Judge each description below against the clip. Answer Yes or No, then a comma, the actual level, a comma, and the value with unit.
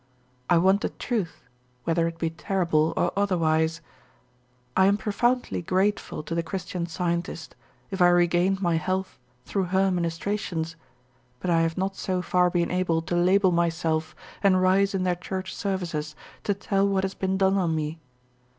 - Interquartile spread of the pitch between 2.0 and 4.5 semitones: Yes, narrow, 2.6 semitones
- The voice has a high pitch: No, medium, 180 Hz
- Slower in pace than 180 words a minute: Yes, average, 165 wpm